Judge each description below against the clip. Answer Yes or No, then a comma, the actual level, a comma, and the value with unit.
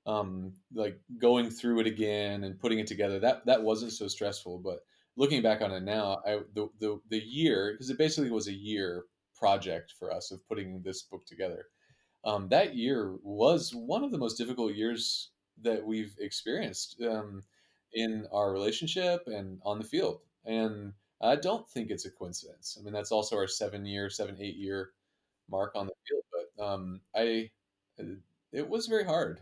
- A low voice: Yes, low, 105 Hz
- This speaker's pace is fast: No, average, 180 wpm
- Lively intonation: No, average, 2.9 semitones